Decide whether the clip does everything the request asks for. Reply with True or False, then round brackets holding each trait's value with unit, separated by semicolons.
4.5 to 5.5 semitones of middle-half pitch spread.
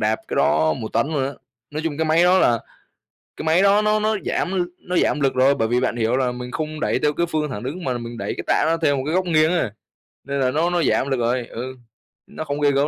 True (4.8 semitones)